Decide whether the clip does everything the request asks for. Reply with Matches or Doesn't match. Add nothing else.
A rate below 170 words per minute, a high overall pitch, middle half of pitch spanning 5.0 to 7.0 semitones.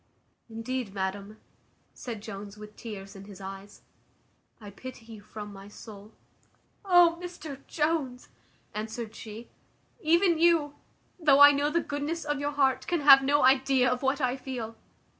Matches